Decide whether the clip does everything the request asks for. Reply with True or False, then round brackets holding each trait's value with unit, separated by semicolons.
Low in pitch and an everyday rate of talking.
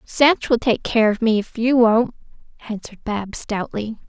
False (225 Hz; 175 wpm)